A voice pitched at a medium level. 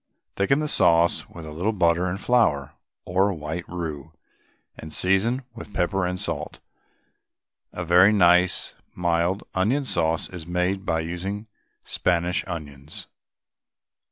No: very low, 90 Hz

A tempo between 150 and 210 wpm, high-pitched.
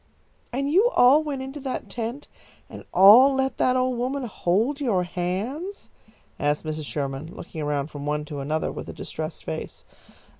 Yes: average, 165 wpm; high, 225 Hz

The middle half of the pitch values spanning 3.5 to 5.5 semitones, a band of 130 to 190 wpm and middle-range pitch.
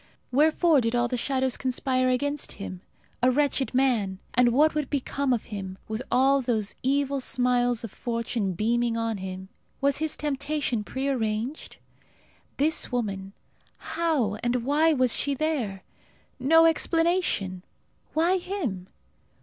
No: average, 4.1 semitones; slow, 135 wpm; very high, 255 Hz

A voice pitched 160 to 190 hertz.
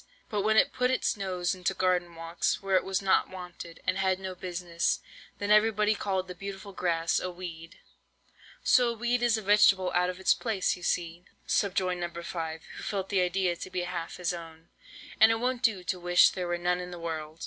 Yes: medium, 185 Hz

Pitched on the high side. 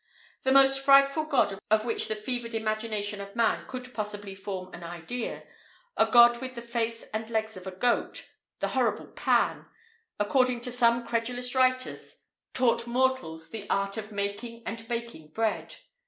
Yes: high, 230 Hz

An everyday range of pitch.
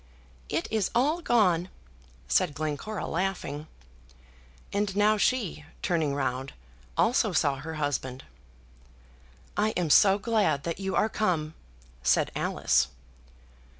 No: wide, 6.2 semitones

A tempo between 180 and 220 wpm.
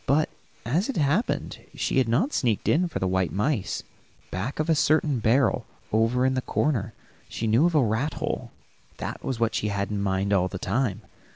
Yes: average, 195 wpm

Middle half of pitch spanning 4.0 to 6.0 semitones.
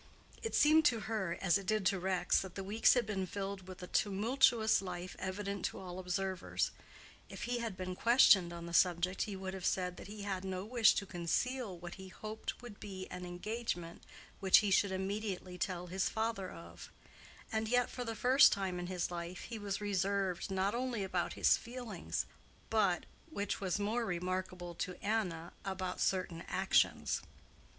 No: average, 2.9 semitones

